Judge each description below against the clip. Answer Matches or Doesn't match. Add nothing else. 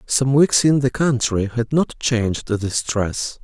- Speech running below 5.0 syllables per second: Matches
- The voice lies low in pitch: Matches